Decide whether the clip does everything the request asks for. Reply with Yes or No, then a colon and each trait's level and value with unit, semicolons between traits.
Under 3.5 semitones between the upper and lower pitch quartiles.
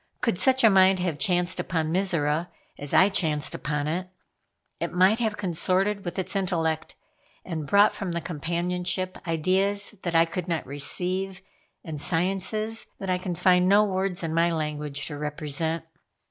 Yes: average, 3.0 semitones